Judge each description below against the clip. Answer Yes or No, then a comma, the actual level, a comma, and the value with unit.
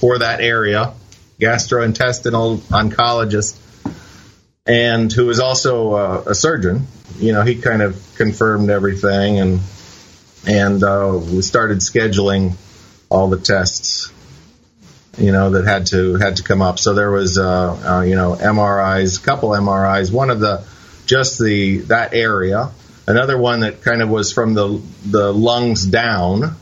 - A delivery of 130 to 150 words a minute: Yes, average, 145 wpm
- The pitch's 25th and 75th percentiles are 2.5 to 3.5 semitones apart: Yes, average, 2.9 semitones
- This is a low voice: Yes, low, 105 Hz